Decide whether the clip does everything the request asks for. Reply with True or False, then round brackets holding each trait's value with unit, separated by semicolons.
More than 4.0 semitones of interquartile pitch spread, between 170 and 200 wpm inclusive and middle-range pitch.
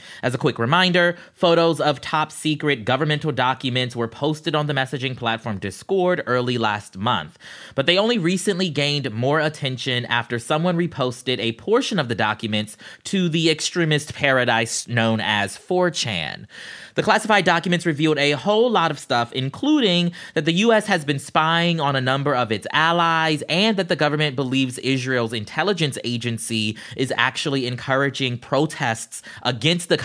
False (5.4 semitones; 155 wpm; 145 Hz)